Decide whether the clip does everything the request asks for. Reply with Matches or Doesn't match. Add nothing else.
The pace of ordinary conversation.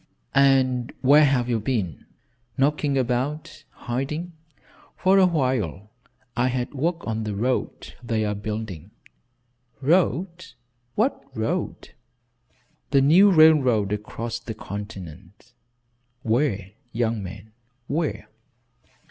Doesn't match